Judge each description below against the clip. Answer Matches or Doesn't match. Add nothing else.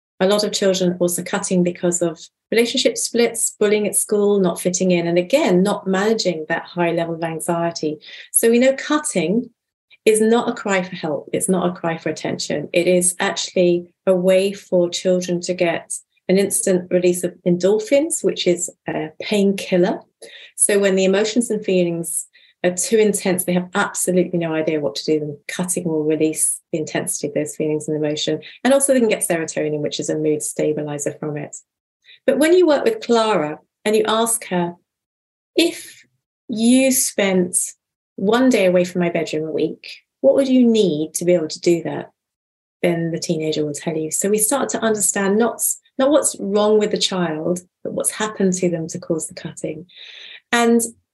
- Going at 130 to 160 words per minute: Doesn't match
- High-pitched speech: Doesn't match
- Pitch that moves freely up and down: Doesn't match